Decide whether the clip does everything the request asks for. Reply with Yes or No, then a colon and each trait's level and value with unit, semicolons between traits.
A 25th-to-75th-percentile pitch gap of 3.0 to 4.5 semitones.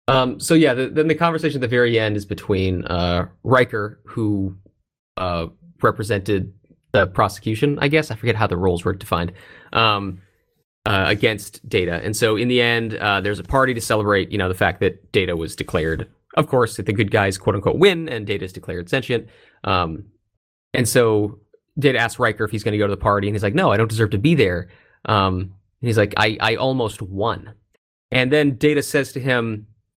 Yes: average, 4.1 semitones